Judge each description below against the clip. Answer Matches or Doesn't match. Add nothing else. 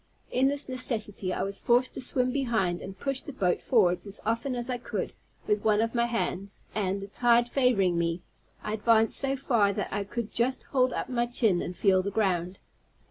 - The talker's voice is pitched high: Matches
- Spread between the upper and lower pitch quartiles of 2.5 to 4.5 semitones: Matches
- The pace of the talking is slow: Doesn't match